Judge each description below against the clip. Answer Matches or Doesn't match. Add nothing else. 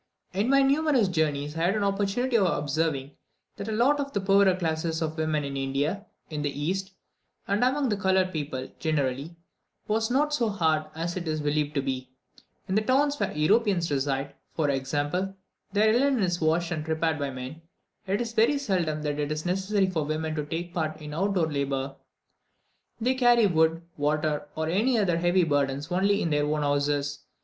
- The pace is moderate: Matches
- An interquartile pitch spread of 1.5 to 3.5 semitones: Doesn't match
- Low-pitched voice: Doesn't match